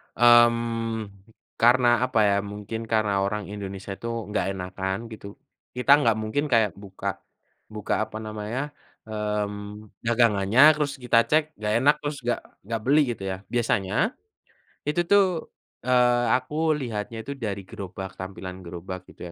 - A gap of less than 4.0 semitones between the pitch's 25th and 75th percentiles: Yes, average, 3.5 semitones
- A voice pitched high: No, low, 110 Hz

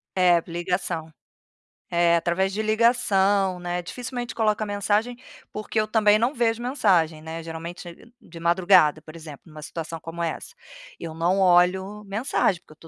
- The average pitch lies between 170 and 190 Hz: Yes, medium, 185 Hz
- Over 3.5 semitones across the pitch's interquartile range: Yes, average, 4.1 semitones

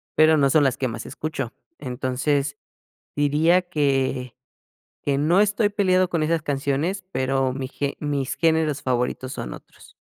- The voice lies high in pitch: No, medium, 145 Hz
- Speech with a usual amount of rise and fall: Yes, average, 3.3 semitones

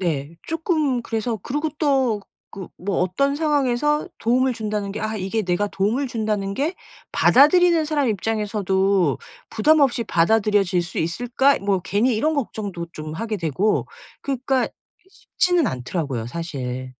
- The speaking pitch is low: No, high, 215 Hz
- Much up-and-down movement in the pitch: Yes, wide, 6.5 semitones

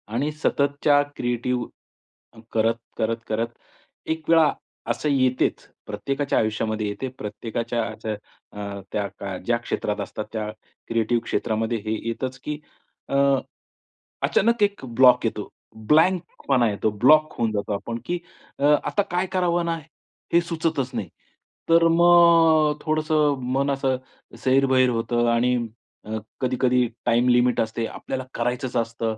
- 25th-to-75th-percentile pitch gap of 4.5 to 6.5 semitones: Yes, average, 4.9 semitones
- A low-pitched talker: Yes, low, 125 Hz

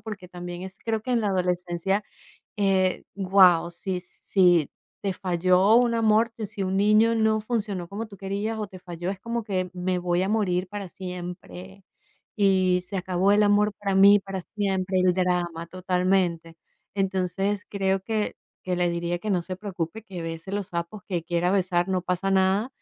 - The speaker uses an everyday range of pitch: No, narrow, 2.2 semitones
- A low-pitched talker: No, high, 190 Hz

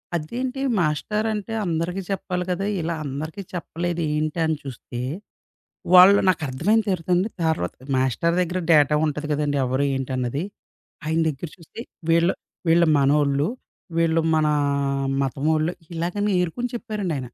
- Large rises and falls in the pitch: No, average, 3.5 semitones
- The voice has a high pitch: No, medium, 165 Hz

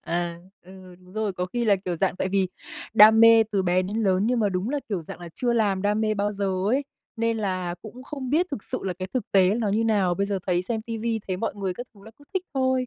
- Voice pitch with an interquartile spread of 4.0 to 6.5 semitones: No, average, 3.5 semitones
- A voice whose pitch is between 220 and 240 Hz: No, high, 205 Hz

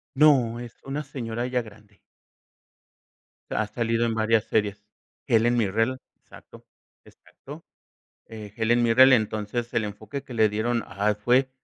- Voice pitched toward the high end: No, low, 115 Hz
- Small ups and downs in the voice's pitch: Yes, narrow, 2.2 semitones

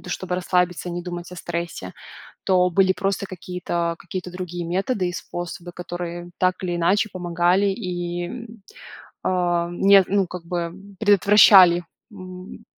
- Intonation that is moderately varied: No, narrow, 1.3 semitones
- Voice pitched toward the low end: No, medium, 180 Hz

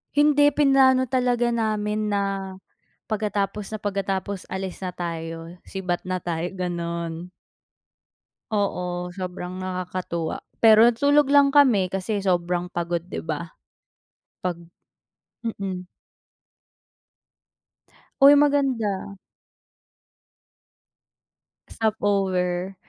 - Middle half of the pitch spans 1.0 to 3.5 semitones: No, average, 4.0 semitones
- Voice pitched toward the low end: No, high, 195 Hz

